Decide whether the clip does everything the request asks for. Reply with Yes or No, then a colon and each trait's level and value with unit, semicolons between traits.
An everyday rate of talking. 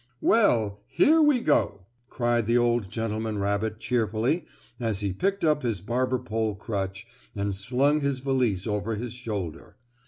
Yes: average, 150 wpm